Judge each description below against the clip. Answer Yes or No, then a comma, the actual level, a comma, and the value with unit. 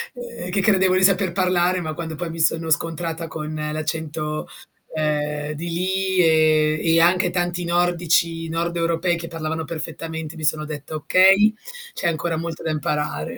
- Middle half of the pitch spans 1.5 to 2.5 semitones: Yes, narrow, 2.2 semitones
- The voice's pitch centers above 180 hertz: No, medium, 165 Hz